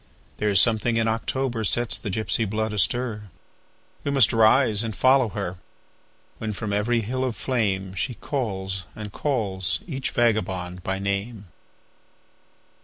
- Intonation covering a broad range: No, average, 3.5 semitones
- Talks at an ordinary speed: No, slow, 125 wpm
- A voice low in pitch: Yes, low, 110 Hz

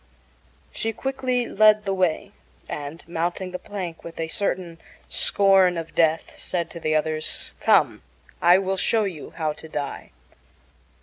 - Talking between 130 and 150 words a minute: Yes, average, 145 wpm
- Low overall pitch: No, medium, 175 Hz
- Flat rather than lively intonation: No, average, 3.3 semitones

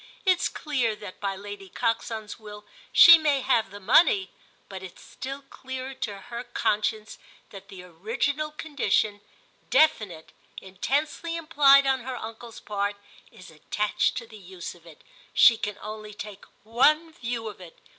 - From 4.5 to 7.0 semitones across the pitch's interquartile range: Yes, average, 5.1 semitones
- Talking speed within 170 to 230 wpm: No, average, 150 wpm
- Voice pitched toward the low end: No, high, 220 Hz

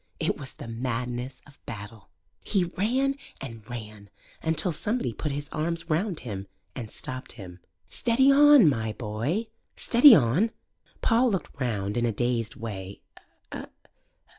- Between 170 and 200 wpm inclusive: No, average, 140 wpm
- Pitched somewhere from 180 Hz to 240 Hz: No, low, 130 Hz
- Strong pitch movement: Yes, wide, 8.7 semitones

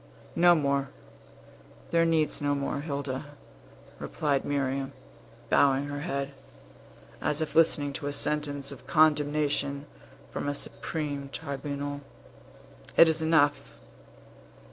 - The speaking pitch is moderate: Yes, medium, 145 Hz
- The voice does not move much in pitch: Yes, narrow, 1.5 semitones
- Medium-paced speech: No, slow, 110 wpm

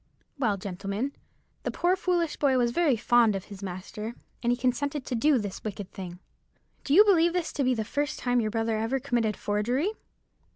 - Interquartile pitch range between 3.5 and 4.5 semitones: No, average, 5.2 semitones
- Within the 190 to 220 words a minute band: Yes, average, 195 wpm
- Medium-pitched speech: No, high, 240 Hz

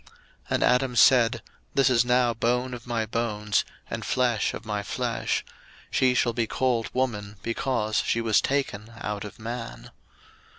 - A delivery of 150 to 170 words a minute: Yes, average, 160 wpm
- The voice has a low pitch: Yes, low, 115 Hz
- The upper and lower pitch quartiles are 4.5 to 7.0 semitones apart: No, narrow, 2.4 semitones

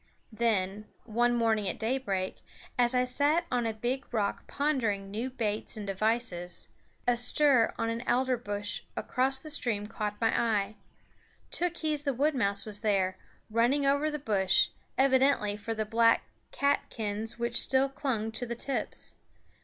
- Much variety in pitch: No, average, 4.0 semitones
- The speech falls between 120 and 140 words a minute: No, average, 155 wpm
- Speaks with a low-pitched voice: No, high, 230 Hz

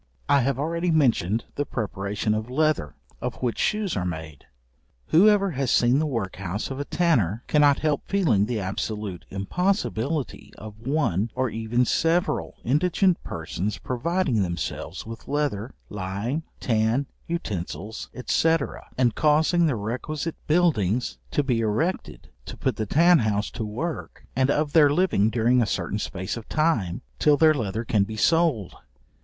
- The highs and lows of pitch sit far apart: Yes, wide, 6.8 semitones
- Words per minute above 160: No, average, 150 wpm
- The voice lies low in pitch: Yes, low, 125 Hz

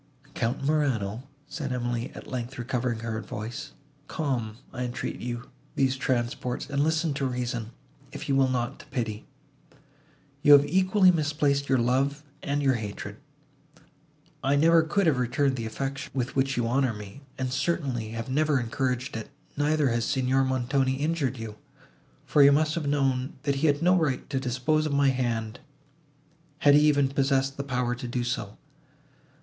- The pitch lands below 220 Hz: Yes, low, 135 Hz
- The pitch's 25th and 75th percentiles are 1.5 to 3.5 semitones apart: Yes, average, 2.9 semitones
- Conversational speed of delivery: Yes, average, 165 wpm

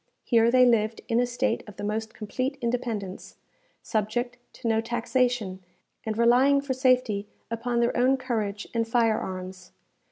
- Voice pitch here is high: Yes, high, 235 Hz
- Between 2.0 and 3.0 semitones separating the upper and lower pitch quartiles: Yes, narrow, 2.5 semitones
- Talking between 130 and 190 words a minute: Yes, average, 155 wpm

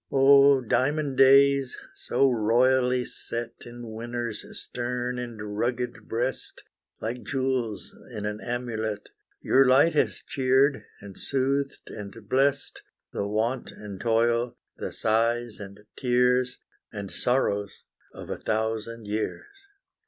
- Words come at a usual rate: No, slow, 115 wpm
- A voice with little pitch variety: No, average, 3.0 semitones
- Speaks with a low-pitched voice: Yes, low, 120 Hz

